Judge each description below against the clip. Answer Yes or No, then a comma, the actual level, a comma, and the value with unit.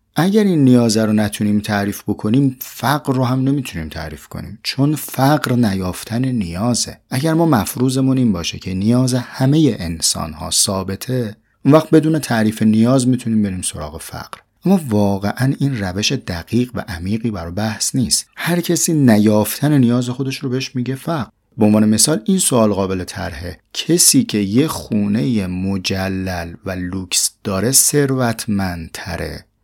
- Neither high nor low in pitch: No, low, 115 Hz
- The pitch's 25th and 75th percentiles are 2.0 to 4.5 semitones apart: No, average, 5.1 semitones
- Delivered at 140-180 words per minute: Yes, average, 145 wpm